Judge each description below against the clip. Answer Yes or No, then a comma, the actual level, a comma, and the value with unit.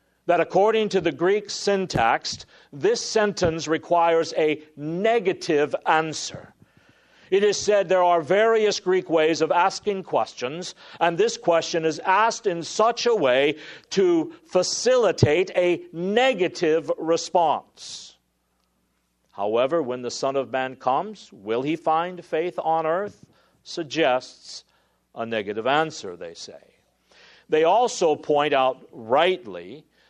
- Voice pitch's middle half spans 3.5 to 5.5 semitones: Yes, average, 4.8 semitones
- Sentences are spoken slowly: Yes, slow, 120 wpm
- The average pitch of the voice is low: No, medium, 175 Hz